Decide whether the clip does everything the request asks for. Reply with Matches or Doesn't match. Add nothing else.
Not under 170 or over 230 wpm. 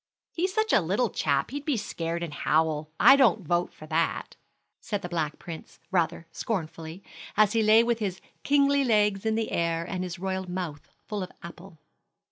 Matches